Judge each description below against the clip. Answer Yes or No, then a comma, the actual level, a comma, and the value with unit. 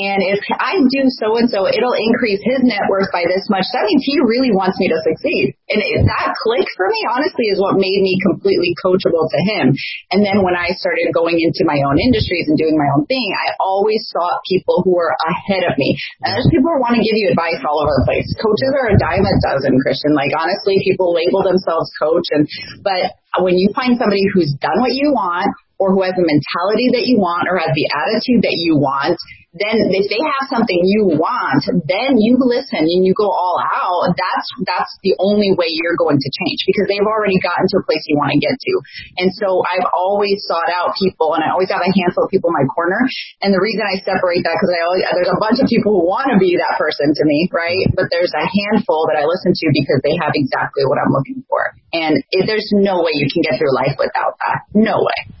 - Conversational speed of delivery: No, fast, 235 wpm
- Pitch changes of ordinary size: Yes, average, 4.1 semitones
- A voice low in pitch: No, high, 190 Hz